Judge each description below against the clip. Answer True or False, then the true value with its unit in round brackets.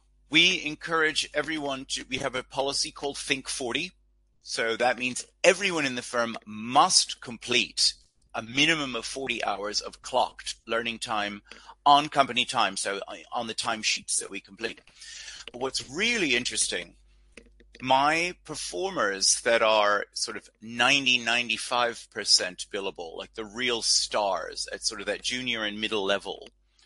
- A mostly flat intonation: False (4.1 semitones)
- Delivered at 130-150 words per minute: True (140 wpm)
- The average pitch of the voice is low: True (125 Hz)